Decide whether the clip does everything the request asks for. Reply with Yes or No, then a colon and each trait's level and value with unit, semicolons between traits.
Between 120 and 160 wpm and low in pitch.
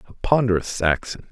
Yes: slow, 135 wpm; low, 105 Hz